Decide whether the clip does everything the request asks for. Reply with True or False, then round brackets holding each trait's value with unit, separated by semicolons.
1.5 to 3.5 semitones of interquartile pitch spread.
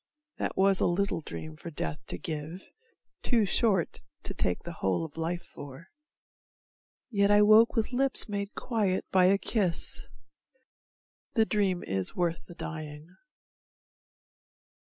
False (4.2 semitones)